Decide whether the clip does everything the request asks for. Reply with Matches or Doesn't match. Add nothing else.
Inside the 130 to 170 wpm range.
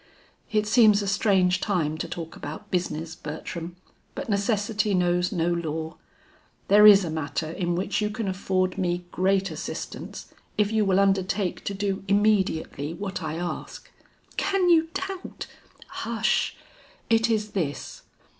Matches